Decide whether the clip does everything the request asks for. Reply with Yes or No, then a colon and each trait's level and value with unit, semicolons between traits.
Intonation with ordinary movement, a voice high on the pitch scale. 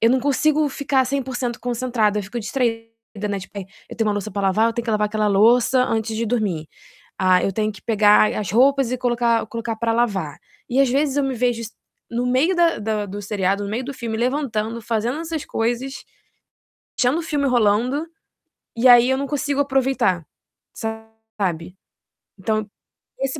Yes: average, 3.6 semitones; high, 230 Hz